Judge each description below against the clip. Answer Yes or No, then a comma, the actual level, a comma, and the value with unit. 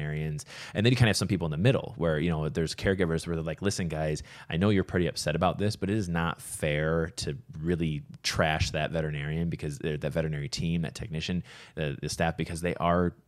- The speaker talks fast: Yes, fast, 230 wpm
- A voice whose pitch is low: Yes, very low, 85 Hz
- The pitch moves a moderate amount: Yes, average, 3.4 semitones